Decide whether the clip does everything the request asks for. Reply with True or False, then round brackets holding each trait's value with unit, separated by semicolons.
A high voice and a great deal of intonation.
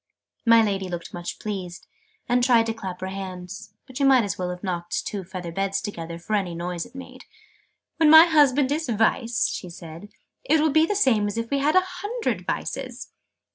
True (210 Hz; 7.0 semitones)